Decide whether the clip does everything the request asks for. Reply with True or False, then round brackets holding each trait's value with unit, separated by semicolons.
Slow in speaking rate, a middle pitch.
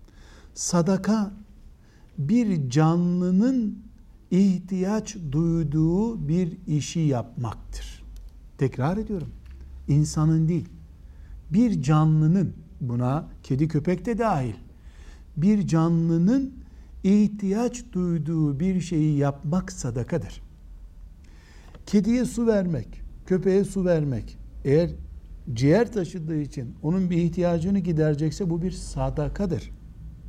True (85 wpm; 160 Hz)